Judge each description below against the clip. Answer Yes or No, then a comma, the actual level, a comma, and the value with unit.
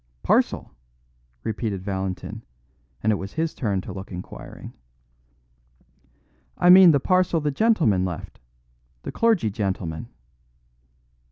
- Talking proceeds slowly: Yes, slow, 110 wpm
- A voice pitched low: Yes, low, 105 Hz